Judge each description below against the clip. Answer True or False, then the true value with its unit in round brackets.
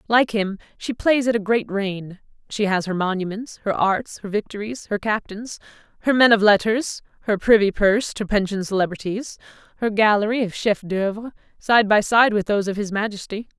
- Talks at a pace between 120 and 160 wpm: False (180 wpm)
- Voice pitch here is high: True (210 Hz)